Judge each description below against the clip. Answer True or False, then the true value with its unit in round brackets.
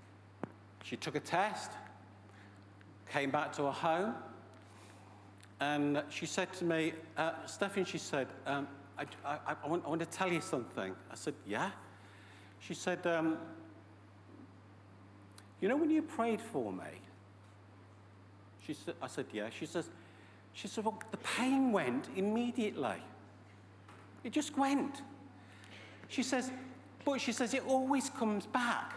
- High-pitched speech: False (140 Hz)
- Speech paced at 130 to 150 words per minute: True (140 wpm)